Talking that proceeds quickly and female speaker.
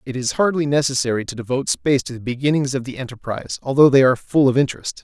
No: fast, 225 wpm; male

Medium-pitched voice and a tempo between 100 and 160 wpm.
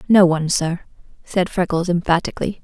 Yes: medium, 175 Hz; slow, 135 wpm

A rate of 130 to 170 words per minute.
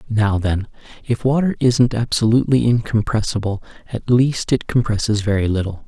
Yes: slow, 135 wpm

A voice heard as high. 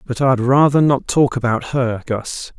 No: low, 130 Hz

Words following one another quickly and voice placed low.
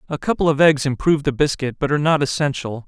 No: fast, 230 wpm; medium, 145 Hz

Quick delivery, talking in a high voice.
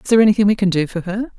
Yes: fast, 345 wpm; high, 200 Hz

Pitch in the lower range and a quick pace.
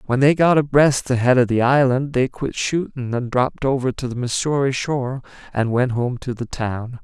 Yes: low, 130 Hz; fast, 215 wpm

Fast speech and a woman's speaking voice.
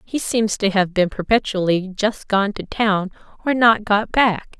No: average, 185 wpm; female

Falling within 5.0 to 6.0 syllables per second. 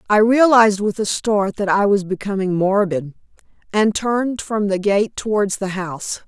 No: 4.8 syllables/s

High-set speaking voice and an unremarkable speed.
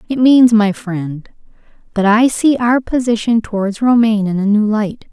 Yes: high, 220 Hz; average, 175 wpm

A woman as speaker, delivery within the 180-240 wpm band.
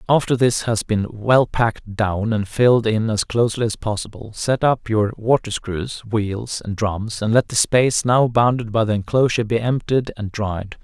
No: male; average, 195 wpm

